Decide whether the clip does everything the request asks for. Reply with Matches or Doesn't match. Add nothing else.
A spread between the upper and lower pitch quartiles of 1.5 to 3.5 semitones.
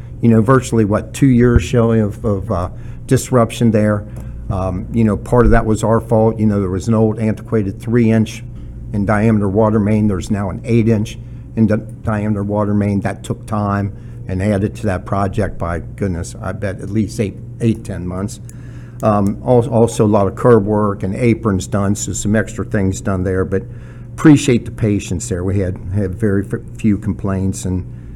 Matches